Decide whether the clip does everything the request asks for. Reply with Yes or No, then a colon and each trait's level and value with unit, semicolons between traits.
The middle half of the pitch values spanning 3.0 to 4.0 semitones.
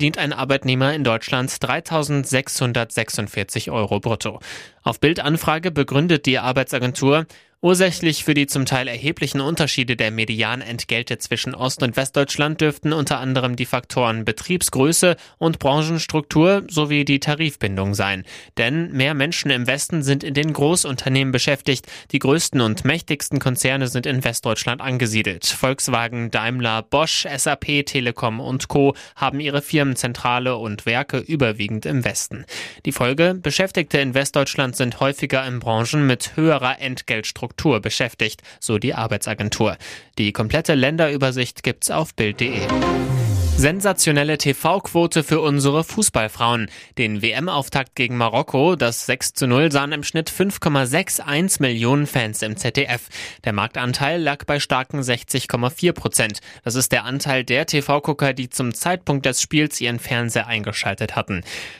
Yes: average, 3.7 semitones